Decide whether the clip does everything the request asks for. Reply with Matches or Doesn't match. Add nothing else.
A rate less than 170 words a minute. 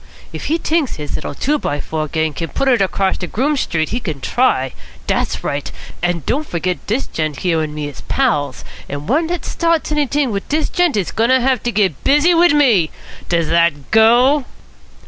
Doesn't match